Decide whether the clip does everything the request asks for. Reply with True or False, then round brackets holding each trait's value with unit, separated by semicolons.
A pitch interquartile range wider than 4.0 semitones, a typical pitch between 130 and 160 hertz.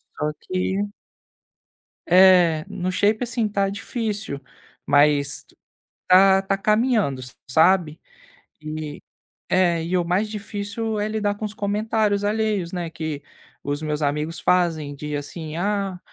False (4.8 semitones; 185 Hz)